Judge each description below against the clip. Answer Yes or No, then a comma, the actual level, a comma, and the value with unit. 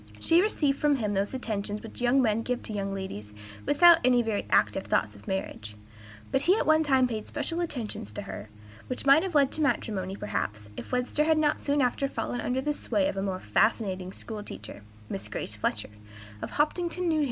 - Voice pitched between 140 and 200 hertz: No, high, 240 Hz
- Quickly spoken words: Yes, fast, 210 wpm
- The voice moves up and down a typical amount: No, wide, 7.0 semitones